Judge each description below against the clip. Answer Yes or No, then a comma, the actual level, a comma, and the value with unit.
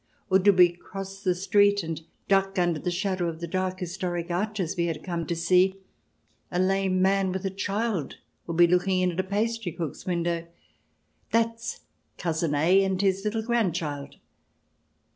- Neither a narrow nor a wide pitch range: No, narrow, 2.3 semitones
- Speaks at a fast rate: No, average, 180 wpm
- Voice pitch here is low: No, medium, 185 Hz